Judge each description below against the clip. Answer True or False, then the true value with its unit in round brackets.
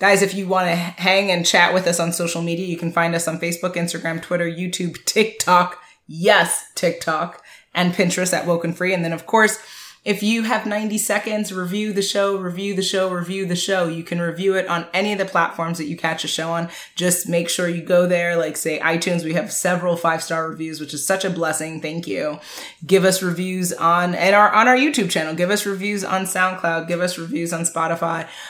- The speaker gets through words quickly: True (220 wpm)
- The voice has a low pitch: False (175 Hz)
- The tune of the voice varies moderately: False (2.3 semitones)